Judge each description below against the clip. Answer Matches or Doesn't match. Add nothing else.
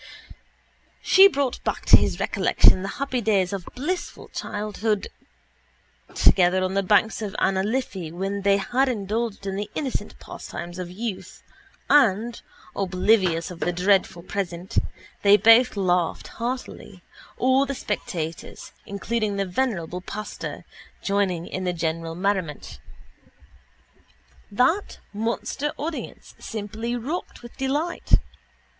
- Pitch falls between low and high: Doesn't match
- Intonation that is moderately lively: Matches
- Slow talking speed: Matches